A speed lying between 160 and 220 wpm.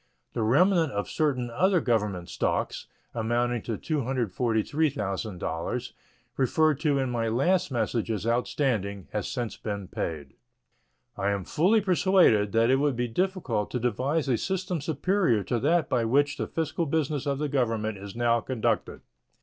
No: average, 150 wpm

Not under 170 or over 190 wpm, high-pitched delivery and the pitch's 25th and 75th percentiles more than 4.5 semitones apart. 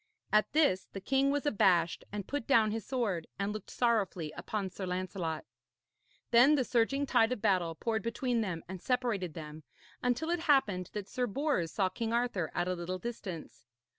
Yes: average, 180 wpm; high, 210 Hz; average, 5.3 semitones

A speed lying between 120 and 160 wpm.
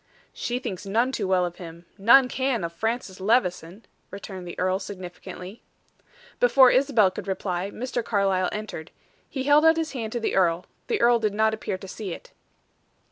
No: average, 180 wpm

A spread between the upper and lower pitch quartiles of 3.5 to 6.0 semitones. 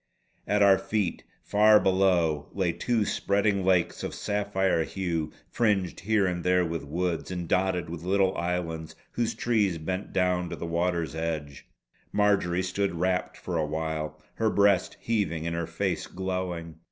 No: average, 3.0 semitones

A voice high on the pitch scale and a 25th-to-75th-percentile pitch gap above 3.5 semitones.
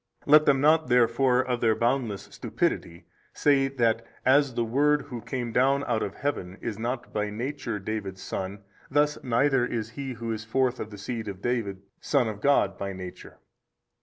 No: low, 120 Hz; average, 3.9 semitones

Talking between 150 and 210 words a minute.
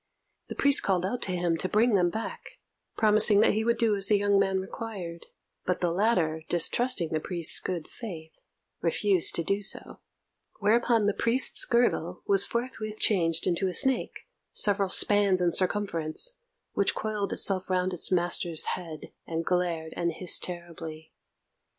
Yes: average, 160 wpm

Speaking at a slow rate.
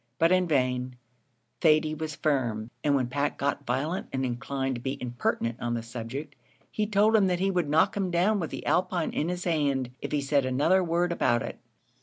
No: fast, 205 wpm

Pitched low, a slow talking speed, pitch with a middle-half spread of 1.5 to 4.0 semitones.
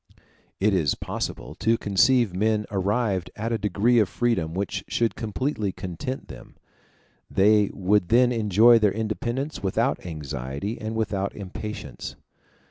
Yes: low, 105 Hz; slow, 130 wpm; average, 3.3 semitones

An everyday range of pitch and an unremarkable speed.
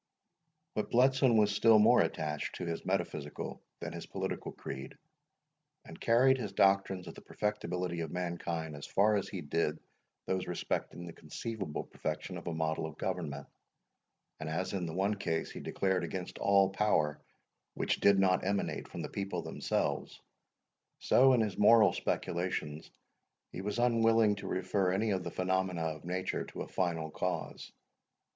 Yes: average, 3.9 semitones; average, 160 wpm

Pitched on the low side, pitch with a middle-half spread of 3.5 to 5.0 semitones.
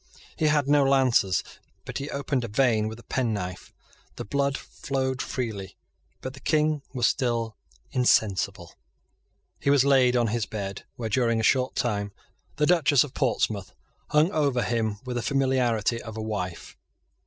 Yes: low, 125 Hz; average, 3.9 semitones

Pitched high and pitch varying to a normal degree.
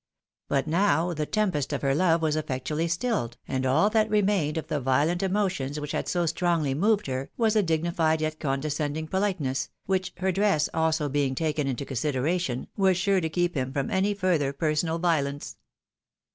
No: medium, 160 Hz; average, 4.6 semitones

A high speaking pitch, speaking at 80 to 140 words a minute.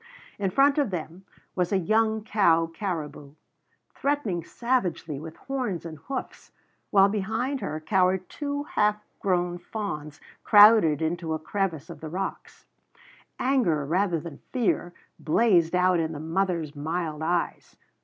No: medium, 180 Hz; slow, 135 wpm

